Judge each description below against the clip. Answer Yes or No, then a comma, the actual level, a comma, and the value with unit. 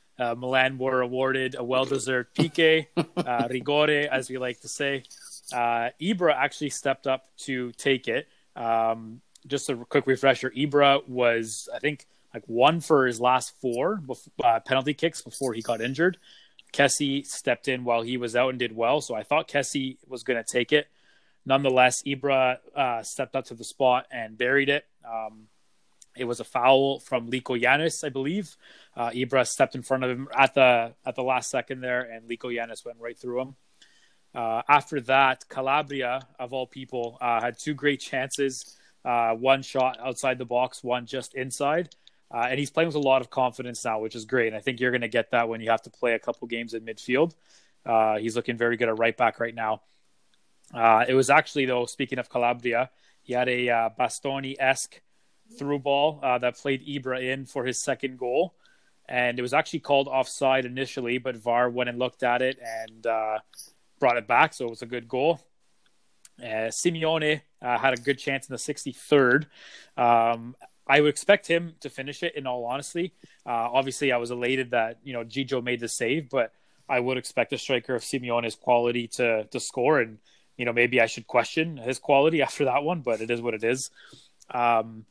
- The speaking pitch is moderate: No, low, 130 Hz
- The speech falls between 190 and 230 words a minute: Yes, average, 200 wpm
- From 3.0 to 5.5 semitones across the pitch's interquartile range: No, narrow, 2.4 semitones